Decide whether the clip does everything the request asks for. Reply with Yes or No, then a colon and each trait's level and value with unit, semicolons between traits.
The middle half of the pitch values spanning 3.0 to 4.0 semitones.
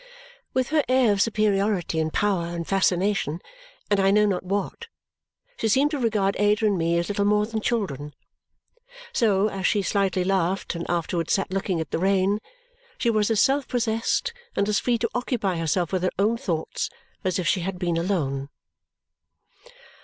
Yes: average, 3.4 semitones